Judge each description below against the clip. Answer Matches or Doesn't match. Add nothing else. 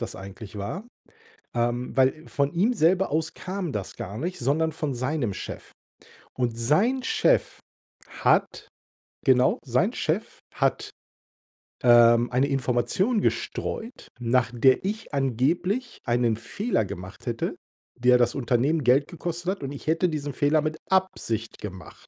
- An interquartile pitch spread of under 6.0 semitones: Doesn't match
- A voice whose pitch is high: Doesn't match